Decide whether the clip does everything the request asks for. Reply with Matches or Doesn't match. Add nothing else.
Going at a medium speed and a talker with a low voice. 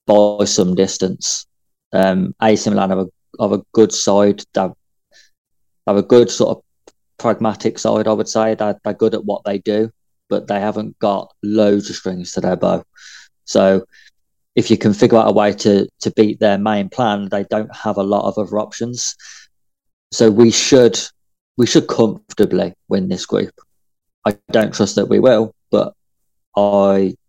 Matches